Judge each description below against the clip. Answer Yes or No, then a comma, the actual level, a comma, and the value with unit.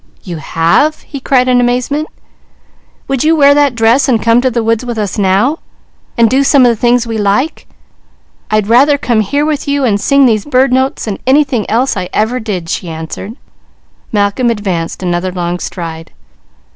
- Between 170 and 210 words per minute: Yes, average, 185 wpm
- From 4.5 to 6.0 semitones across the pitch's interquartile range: Yes, average, 4.9 semitones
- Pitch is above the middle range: Yes, high, 235 Hz